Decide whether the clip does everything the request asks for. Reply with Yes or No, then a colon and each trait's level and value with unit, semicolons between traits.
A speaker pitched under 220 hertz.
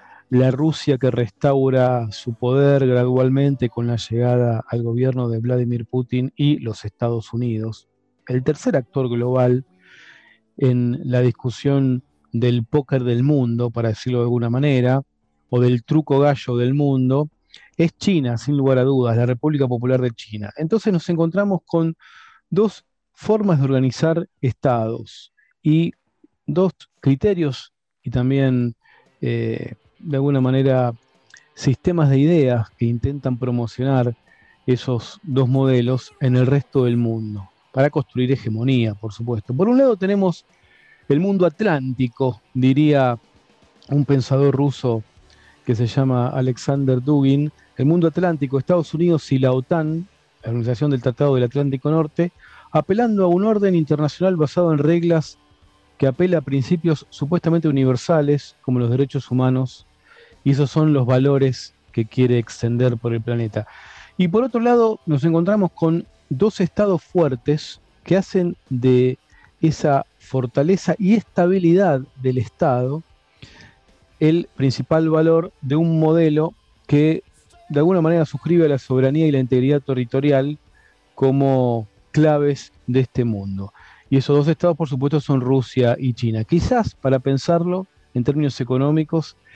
Yes: low, 135 Hz